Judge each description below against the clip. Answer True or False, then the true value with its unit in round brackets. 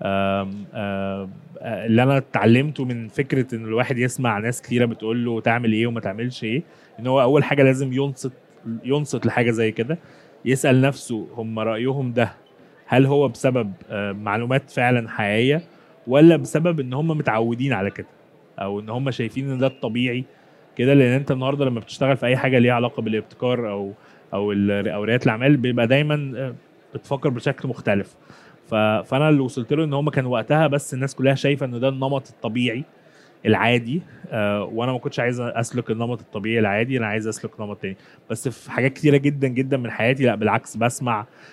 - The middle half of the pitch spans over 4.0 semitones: False (3.3 semitones)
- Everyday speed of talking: False (170 wpm)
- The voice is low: True (125 Hz)